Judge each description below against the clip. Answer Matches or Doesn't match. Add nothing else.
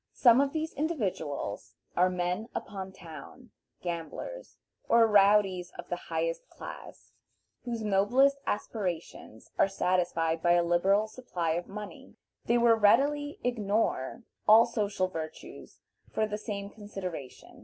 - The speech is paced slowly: Matches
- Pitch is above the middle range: Matches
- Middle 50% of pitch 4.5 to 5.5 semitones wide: Matches